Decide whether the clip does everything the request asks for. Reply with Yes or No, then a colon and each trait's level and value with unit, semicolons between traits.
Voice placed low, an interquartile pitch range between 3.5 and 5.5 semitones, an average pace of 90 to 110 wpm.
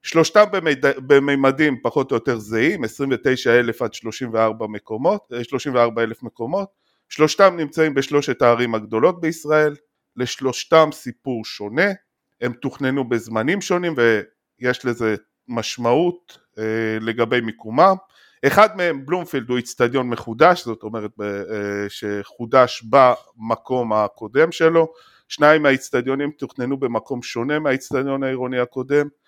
Yes: low, 130 Hz; average, 4.8 semitones; average, 105 wpm